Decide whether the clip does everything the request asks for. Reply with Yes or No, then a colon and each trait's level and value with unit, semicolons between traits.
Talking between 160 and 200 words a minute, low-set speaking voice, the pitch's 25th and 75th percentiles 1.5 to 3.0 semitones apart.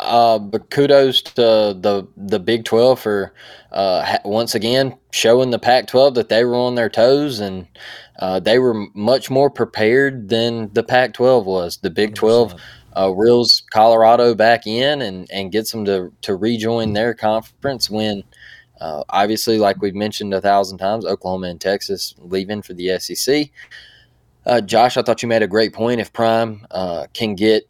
Yes: average, 175 wpm; low, 110 Hz; average, 2.7 semitones